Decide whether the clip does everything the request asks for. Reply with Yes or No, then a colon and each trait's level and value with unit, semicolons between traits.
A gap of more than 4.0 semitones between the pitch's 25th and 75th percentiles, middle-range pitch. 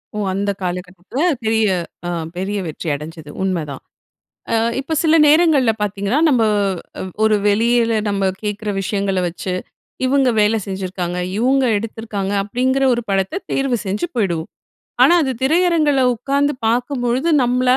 No: wide, 5.5 semitones; high, 220 Hz